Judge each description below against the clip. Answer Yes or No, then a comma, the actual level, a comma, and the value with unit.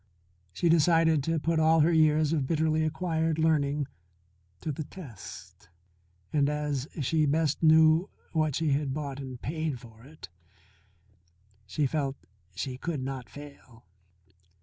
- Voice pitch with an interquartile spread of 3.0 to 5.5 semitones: No, narrow, 2.5 semitones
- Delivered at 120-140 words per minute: Yes, slow, 135 wpm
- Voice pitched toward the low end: No, medium, 150 Hz